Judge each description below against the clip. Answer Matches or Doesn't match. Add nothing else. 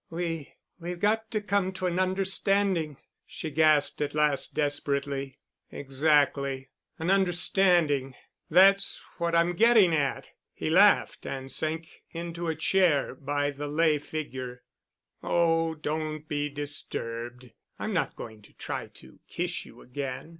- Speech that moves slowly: Matches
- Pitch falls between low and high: Matches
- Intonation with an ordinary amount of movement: Matches